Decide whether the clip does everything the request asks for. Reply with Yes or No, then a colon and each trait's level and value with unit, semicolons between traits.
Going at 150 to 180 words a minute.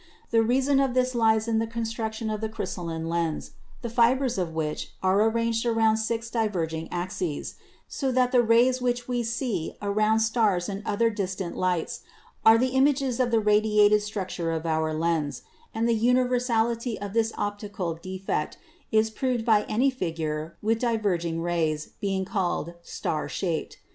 Yes: average, 160 wpm